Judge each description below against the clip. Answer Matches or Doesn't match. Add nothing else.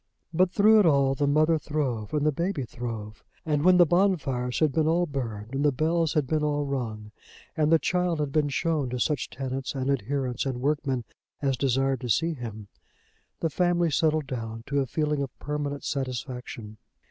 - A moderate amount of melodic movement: Matches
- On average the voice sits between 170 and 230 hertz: Doesn't match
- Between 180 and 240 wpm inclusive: Matches